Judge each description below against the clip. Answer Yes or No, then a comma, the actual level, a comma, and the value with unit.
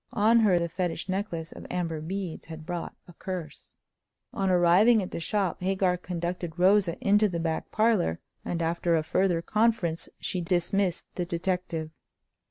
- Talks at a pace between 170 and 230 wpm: No, average, 160 wpm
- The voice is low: No, medium, 180 Hz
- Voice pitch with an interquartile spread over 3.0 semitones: No, narrow, 2.5 semitones